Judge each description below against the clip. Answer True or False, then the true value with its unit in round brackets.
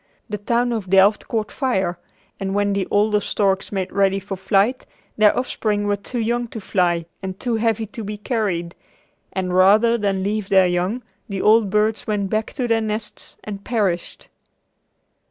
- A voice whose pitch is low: False (205 Hz)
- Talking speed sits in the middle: True (170 wpm)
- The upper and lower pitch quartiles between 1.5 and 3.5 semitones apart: True (2.5 semitones)